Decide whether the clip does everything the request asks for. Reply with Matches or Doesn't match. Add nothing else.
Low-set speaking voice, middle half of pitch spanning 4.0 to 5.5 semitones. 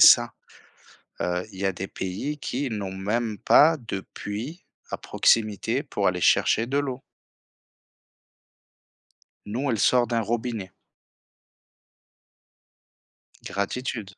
Matches